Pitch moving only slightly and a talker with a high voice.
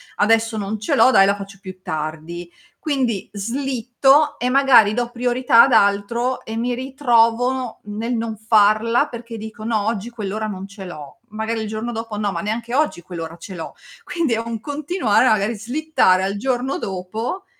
No: average, 3.3 semitones; high, 225 Hz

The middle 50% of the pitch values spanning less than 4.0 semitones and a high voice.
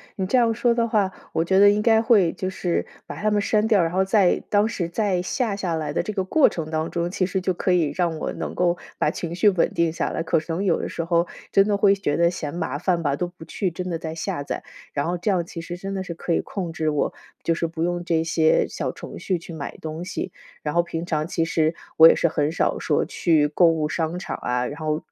No: average, 2.9 semitones; medium, 175 Hz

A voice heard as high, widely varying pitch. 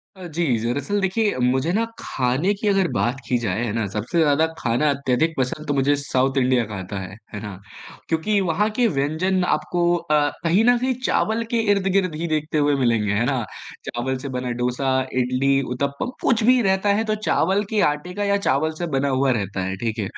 No: medium, 145 Hz; wide, 7.0 semitones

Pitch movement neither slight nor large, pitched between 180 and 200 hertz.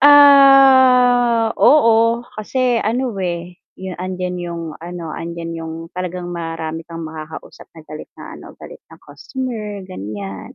No: wide, 6.6 semitones; medium, 185 Hz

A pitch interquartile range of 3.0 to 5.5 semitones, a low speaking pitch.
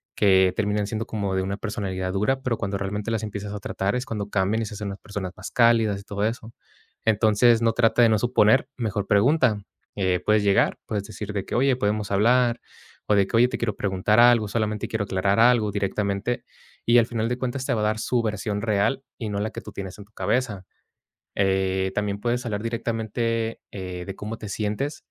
No: narrow, 2.4 semitones; low, 105 Hz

